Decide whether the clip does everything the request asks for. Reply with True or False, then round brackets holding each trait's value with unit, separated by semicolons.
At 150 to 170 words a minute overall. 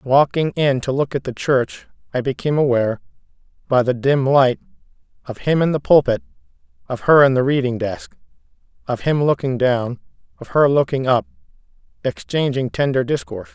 True (160 wpm)